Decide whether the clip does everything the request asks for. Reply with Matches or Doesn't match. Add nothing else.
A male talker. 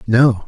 Matches